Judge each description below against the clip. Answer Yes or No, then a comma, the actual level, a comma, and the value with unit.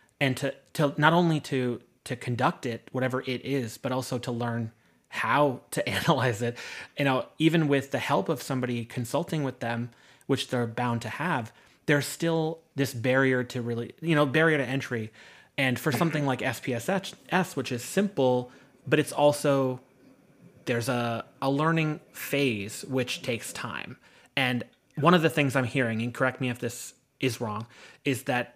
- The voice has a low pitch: Yes, low, 130 Hz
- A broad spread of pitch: No, average, 3.1 semitones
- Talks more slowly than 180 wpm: Yes, average, 170 wpm